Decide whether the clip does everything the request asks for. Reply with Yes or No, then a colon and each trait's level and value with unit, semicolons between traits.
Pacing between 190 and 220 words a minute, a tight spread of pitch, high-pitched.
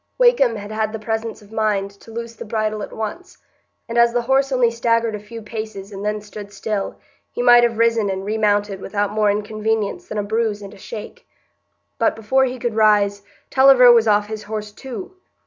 Yes: average, 200 wpm; narrow, 2.1 semitones; high, 220 Hz